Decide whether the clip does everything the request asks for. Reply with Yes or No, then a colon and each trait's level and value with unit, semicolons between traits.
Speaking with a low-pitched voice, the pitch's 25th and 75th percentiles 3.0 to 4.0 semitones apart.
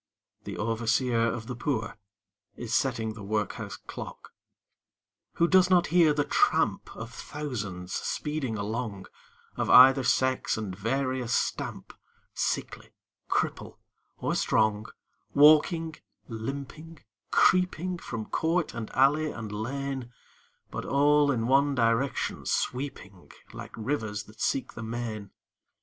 No: low, 125 Hz; average, 4.7 semitones